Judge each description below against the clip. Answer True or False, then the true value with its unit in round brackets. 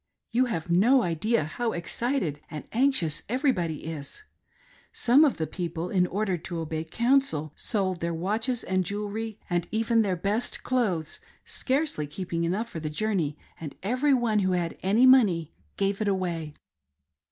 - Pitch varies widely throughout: True (5.9 semitones)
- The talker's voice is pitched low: False (190 Hz)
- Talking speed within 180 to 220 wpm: False (155 wpm)